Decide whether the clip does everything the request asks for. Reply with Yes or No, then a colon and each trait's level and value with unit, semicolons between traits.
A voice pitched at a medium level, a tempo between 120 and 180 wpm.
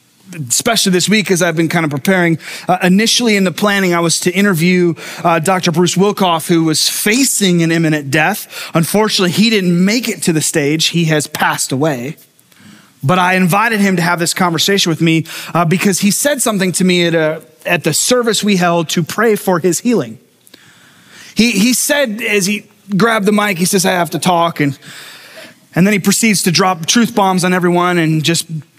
No: medium, 180 Hz; average, 200 wpm